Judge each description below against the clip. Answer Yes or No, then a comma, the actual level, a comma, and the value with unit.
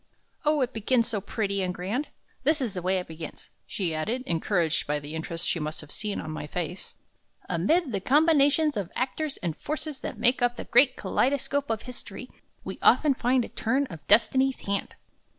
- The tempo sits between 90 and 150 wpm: No, average, 195 wpm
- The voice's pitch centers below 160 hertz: No, high, 225 Hz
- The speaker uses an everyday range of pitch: No, wide, 7.1 semitones